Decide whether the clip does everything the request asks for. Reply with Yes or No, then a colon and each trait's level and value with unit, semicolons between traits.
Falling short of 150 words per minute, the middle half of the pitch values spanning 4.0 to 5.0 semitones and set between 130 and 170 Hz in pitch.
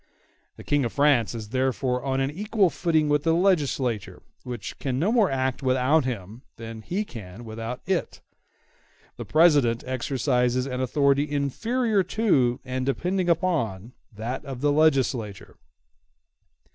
Yes: average, 140 wpm; average, 4.5 semitones; low, 135 Hz